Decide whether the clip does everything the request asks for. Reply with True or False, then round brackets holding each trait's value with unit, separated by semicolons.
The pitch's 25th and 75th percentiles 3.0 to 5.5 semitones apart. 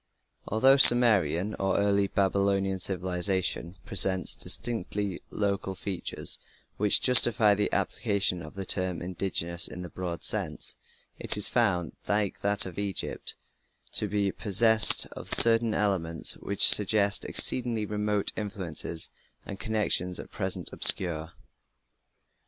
False (2.4 semitones)